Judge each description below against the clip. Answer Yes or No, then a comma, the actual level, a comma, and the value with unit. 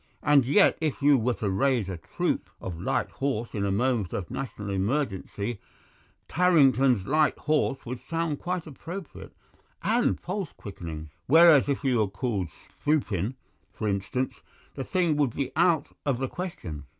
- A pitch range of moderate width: No, wide, 7.3 semitones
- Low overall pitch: Yes, low, 130 Hz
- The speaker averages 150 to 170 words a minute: Yes, average, 155 wpm